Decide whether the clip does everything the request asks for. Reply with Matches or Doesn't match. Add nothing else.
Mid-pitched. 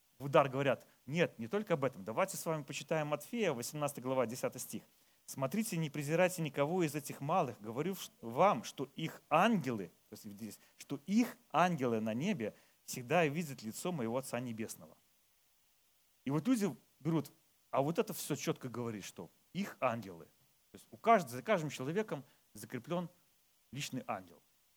Matches